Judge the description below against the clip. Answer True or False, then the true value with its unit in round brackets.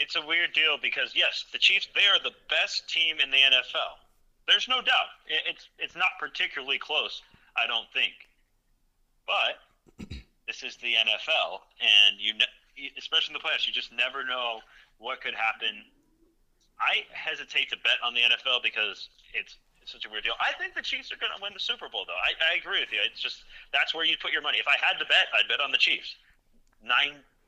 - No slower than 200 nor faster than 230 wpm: True (205 wpm)